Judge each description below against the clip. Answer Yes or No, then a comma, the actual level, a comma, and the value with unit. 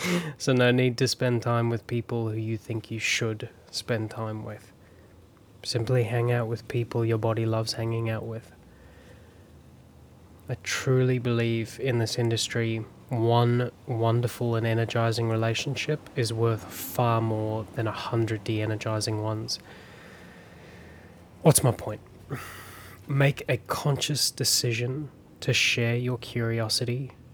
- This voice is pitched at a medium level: No, low, 115 Hz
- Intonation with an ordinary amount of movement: No, narrow, 2.0 semitones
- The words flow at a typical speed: No, slow, 130 wpm